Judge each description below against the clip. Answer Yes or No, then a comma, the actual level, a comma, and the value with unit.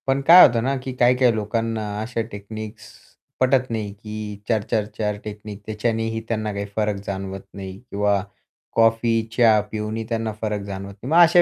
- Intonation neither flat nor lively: No, narrow, 1.8 semitones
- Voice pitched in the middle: No, low, 110 Hz